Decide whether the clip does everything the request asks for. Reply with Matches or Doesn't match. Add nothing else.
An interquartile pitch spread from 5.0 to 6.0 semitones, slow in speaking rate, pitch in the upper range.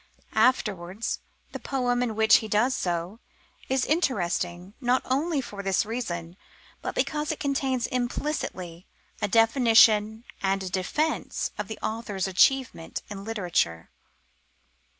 Matches